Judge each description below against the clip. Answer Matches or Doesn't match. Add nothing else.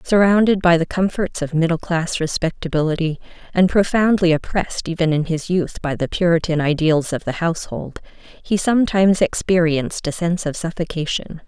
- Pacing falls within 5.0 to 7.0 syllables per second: Matches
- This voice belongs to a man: Doesn't match